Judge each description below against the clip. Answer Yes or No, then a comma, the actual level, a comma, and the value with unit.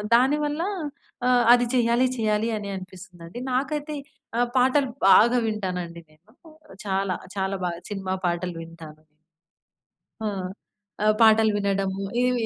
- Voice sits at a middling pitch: No, high, 205 Hz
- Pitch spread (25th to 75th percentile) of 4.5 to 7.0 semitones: Yes, average, 4.9 semitones